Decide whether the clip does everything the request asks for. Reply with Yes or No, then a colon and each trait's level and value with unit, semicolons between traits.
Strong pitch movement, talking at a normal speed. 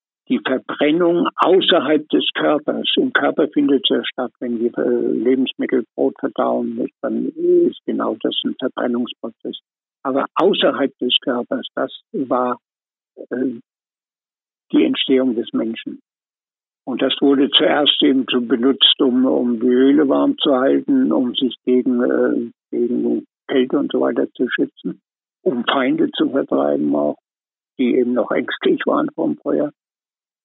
Yes: wide, 6.4 semitones; average, 135 wpm